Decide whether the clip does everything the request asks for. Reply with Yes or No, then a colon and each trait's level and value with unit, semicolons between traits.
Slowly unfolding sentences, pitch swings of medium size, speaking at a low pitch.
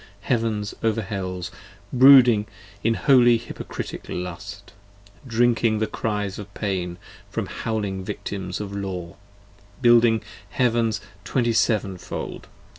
Yes: slow, 110 wpm; average, 3.1 semitones; low, 105 Hz